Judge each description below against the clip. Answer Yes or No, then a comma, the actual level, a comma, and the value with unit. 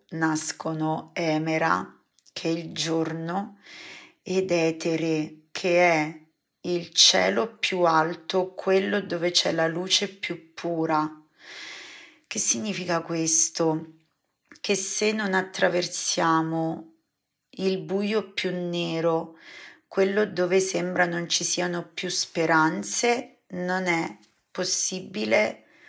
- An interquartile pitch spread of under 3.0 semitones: Yes, narrow, 2.6 semitones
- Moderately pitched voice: Yes, medium, 175 Hz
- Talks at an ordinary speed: No, slow, 100 wpm